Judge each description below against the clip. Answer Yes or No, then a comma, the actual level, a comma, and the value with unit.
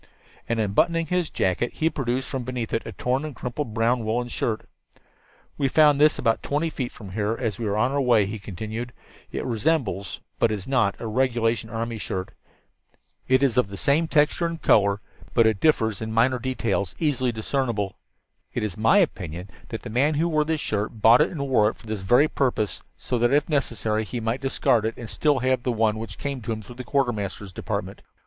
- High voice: No, low, 120 Hz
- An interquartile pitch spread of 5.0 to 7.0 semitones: No, average, 4.0 semitones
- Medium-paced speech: No, fast, 210 wpm